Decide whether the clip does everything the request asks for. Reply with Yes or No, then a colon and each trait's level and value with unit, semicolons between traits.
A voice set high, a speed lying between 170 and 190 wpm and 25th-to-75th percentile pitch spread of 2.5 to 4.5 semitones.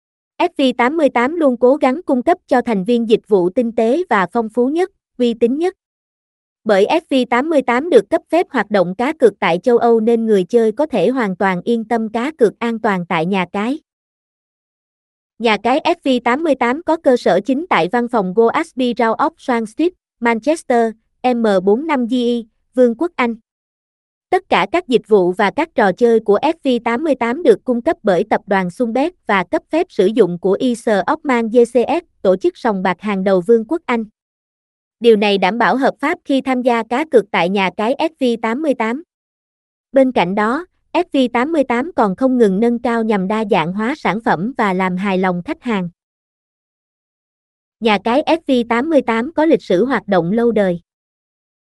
Yes: high, 240 Hz; average, 175 wpm; average, 4.2 semitones